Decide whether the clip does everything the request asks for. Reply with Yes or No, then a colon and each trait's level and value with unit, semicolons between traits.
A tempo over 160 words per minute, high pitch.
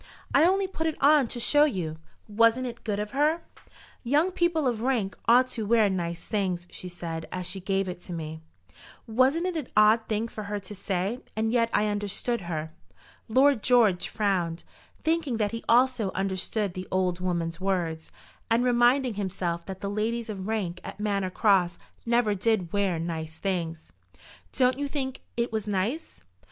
Yes: average, 175 wpm; high, 210 Hz